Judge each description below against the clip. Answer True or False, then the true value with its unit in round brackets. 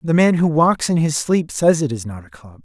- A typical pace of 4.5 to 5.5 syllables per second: True (5.1 syllables/s)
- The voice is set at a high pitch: False (145 Hz)